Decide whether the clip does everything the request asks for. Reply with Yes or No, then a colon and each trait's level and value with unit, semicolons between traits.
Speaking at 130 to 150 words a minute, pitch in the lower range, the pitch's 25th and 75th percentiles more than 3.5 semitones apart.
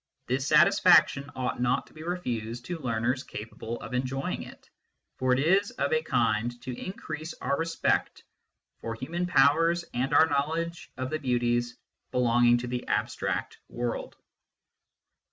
Yes: average, 145 wpm; low, 130 Hz; average, 4.8 semitones